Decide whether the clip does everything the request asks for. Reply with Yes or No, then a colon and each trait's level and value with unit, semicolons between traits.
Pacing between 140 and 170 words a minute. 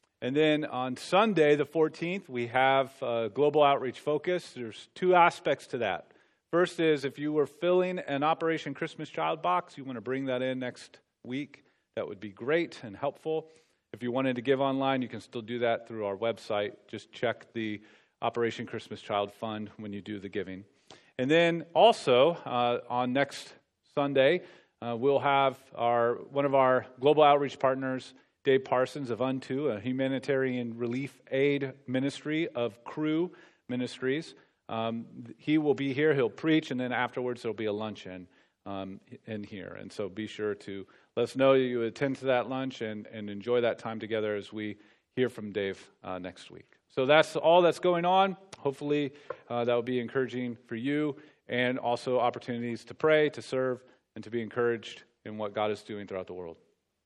No: average, 185 wpm